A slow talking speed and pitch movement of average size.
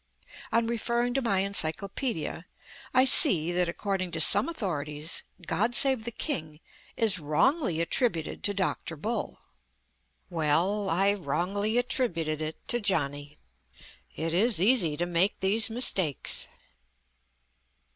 No: slow, 120 wpm; wide, 6.0 semitones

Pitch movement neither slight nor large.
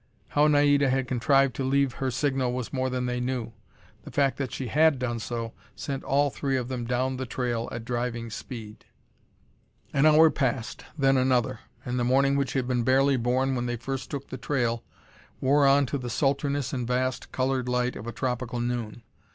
No: narrow, 2.0 semitones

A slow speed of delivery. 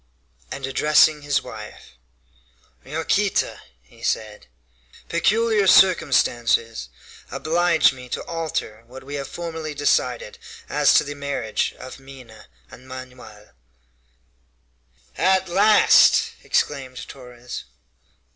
Yes: slow, 100 wpm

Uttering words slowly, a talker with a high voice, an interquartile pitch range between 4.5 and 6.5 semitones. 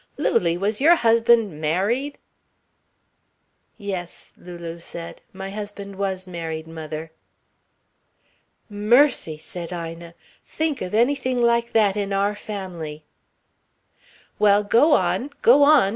Yes: slow, 110 wpm; high, 200 Hz; wide, 5.4 semitones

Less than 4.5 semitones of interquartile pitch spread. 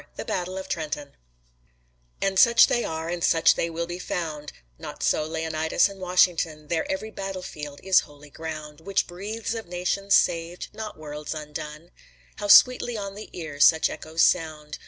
Yes: average, 3.8 semitones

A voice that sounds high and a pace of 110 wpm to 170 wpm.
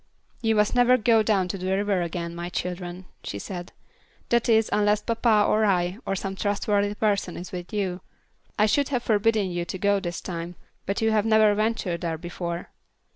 No: high, 200 Hz; average, 190 wpm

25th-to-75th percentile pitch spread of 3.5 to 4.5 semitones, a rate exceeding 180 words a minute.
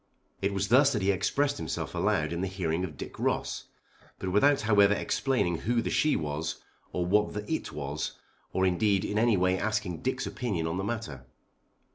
Yes: average, 4.1 semitones; average, 190 wpm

